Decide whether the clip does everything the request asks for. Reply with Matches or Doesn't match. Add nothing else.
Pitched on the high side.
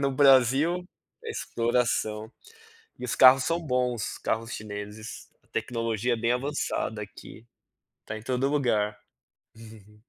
Doesn't match